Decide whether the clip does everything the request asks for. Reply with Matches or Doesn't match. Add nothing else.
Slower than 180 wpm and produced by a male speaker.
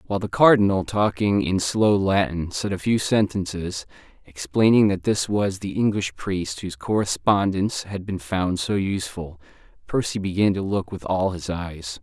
Matches